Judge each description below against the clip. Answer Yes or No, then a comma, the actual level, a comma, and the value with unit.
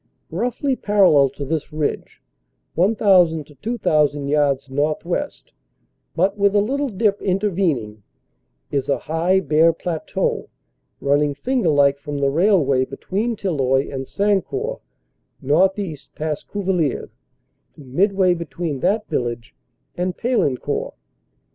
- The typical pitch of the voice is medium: Yes, medium, 165 Hz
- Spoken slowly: Yes, slow, 110 wpm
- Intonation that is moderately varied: No, wide, 5.9 semitones